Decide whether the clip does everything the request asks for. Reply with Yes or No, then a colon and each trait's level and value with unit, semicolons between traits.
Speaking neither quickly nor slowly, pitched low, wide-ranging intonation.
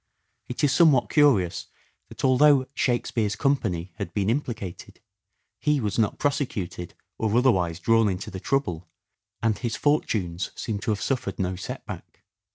Yes: average, 155 wpm; low, 110 Hz; wide, 6.0 semitones